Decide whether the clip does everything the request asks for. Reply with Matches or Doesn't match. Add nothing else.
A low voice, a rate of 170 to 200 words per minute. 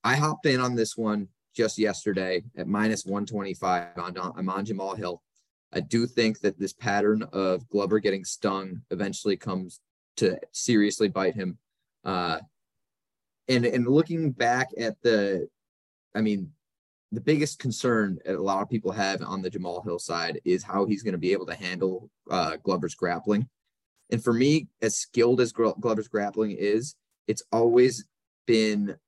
Doesn't match